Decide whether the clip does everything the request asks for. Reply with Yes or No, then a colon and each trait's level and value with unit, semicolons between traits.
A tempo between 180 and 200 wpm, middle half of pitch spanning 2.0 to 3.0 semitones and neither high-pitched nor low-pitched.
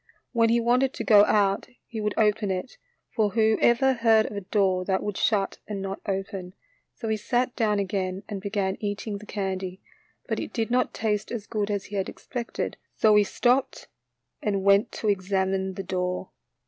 No: average, 190 wpm; narrow, 2.5 semitones; high, 205 Hz